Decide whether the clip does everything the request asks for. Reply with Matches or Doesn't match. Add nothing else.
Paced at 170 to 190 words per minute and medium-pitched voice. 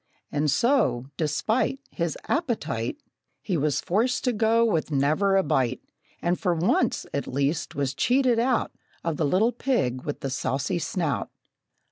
Doesn't match